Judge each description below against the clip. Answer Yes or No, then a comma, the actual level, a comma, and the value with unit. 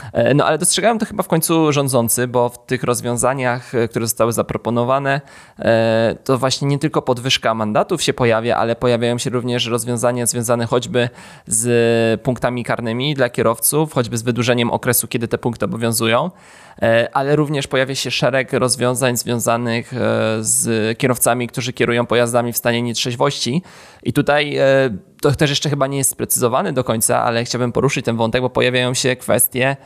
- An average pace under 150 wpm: No, average, 155 wpm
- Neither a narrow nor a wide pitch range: No, narrow, 2.3 semitones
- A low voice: Yes, low, 125 Hz